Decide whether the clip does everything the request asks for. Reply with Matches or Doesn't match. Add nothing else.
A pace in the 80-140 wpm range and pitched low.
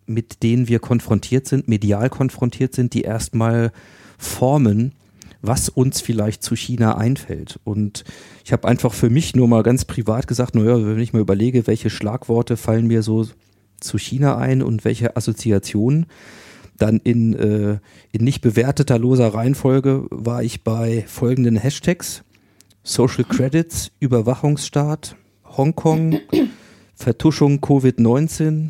Matches